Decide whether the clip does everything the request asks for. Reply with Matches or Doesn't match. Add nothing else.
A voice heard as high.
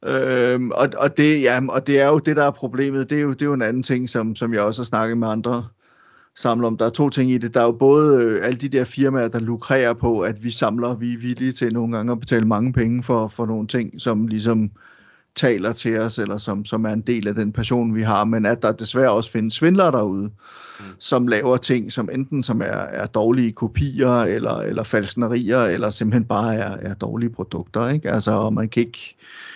Doesn't match